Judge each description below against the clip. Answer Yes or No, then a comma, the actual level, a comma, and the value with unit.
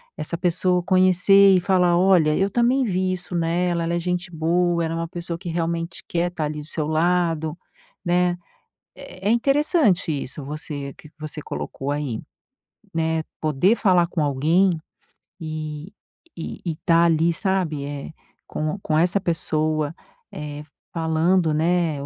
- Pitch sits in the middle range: Yes, medium, 170 Hz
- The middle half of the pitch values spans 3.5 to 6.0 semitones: No, narrow, 2.6 semitones